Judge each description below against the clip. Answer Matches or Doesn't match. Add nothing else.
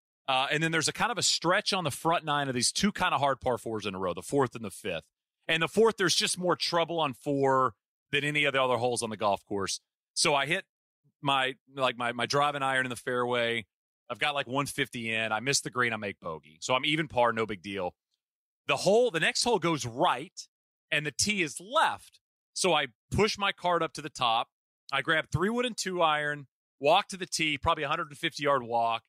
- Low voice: Doesn't match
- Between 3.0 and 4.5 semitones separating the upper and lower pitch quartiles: Doesn't match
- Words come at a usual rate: Doesn't match